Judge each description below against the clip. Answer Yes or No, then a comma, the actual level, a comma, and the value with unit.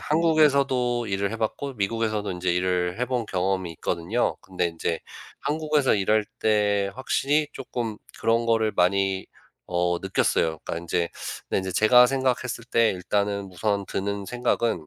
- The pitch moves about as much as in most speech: Yes, average, 4.6 semitones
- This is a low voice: Yes, low, 105 Hz